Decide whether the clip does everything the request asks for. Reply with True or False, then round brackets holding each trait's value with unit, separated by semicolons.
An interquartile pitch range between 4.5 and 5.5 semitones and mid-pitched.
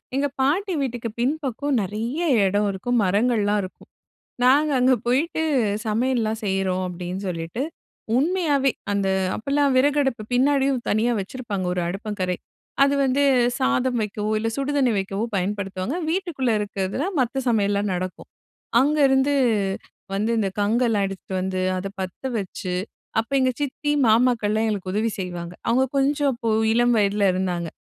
False (5.2 semitones; 230 Hz)